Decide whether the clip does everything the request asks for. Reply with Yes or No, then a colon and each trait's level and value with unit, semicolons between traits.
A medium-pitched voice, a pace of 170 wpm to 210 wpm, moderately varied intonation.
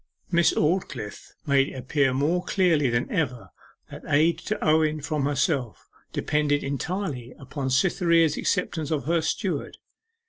No: medium, 150 Hz; slow, 135 wpm; average, 3.5 semitones